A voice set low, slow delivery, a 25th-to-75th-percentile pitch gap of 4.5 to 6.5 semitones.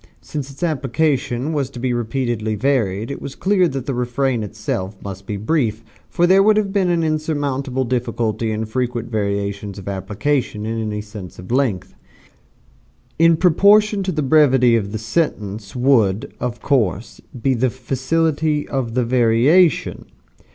No: low, 125 Hz; average, 155 wpm; average, 5.3 semitones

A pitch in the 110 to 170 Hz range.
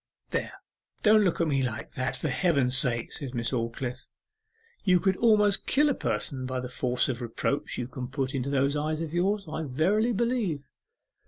Yes: medium, 140 Hz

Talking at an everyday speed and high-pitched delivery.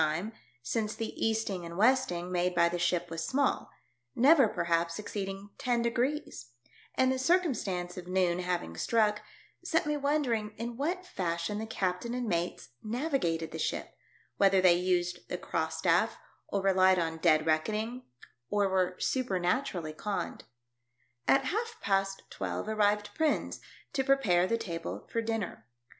Yes: average, 150 wpm; high, 200 Hz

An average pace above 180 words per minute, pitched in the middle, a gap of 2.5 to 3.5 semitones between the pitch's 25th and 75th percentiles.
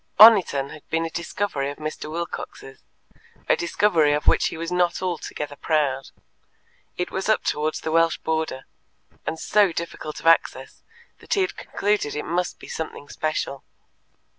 No: average, 160 wpm; medium, 160 Hz; average, 3.0 semitones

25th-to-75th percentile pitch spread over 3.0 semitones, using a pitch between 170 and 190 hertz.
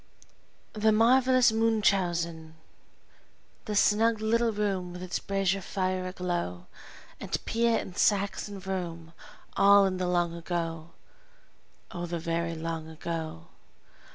Yes: average, 3.7 semitones; medium, 185 Hz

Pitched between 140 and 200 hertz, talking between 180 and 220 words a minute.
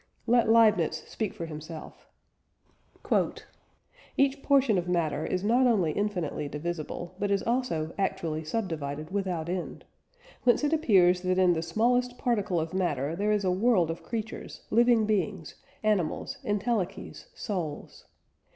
No: high, 190 Hz; slow, 135 wpm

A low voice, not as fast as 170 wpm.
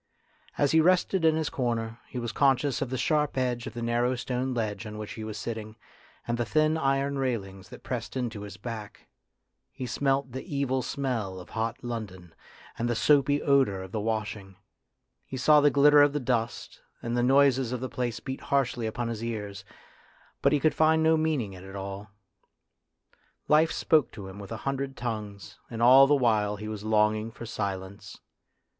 No: low, 120 Hz; average, 190 wpm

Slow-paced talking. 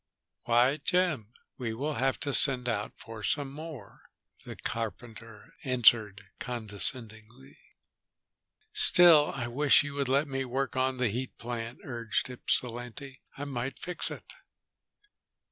Yes: slow, 130 wpm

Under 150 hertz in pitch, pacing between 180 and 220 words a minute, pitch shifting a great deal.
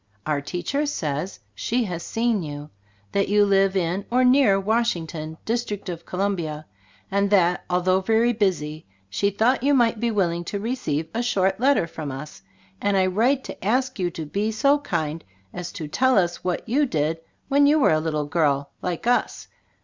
No: high, 195 Hz; average, 185 wpm; wide, 6.2 semitones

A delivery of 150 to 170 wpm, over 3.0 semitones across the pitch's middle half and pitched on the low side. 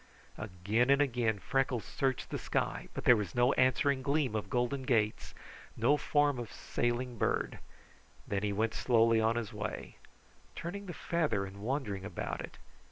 Yes: average, 165 wpm; average, 3.8 semitones; low, 120 Hz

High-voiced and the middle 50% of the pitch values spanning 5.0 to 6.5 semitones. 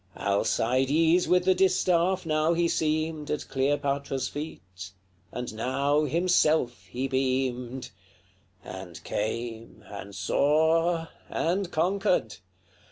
No: medium, 140 Hz; average, 5.3 semitones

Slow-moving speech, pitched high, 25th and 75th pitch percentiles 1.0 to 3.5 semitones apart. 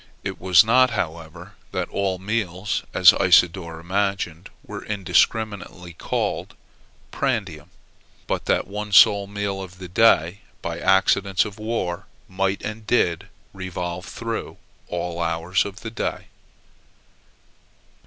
No: slow, 125 wpm; very low, 95 Hz; average, 3.0 semitones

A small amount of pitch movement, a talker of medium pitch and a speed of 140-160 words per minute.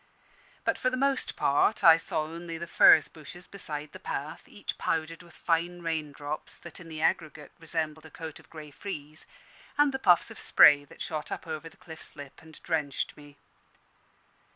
No: narrow, 2.1 semitones; medium, 160 Hz; average, 180 wpm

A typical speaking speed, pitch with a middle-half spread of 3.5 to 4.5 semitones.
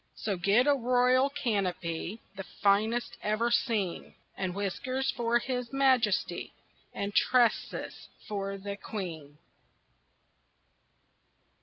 No: slow, 100 wpm; average, 4.0 semitones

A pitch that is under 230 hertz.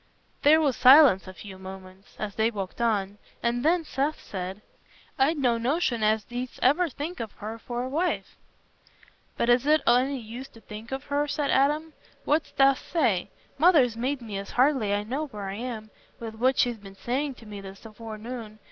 No: high, 240 Hz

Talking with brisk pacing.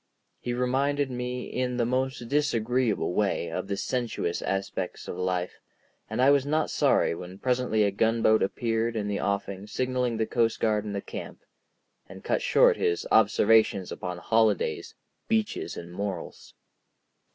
No: average, 150 wpm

